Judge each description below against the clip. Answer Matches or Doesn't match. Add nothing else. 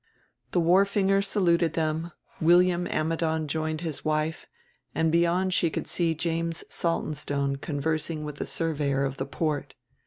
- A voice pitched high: Doesn't match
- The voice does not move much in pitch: Matches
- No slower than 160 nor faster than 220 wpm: Doesn't match